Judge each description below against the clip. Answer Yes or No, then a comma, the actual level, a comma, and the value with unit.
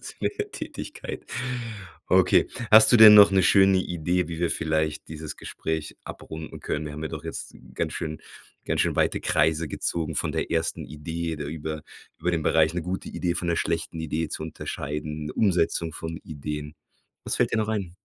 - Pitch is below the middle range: Yes, very low, 80 Hz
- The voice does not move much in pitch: Yes, narrow, 2.3 semitones